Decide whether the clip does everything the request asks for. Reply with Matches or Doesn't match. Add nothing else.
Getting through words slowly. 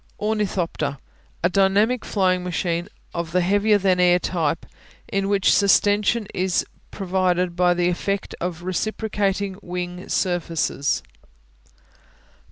Matches